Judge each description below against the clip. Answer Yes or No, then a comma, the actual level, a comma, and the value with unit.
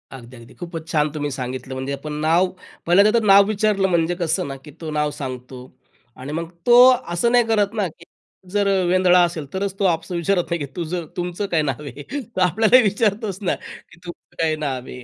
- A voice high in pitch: No, medium, 170 Hz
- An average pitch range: Yes, average, 4.8 semitones